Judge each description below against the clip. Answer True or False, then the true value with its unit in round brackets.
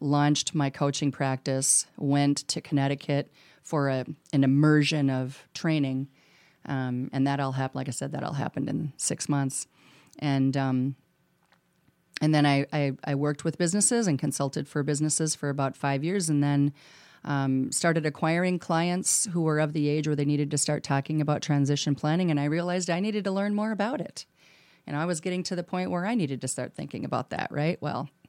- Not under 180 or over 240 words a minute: True (195 wpm)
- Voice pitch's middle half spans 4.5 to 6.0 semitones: False (2.6 semitones)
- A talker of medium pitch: True (145 Hz)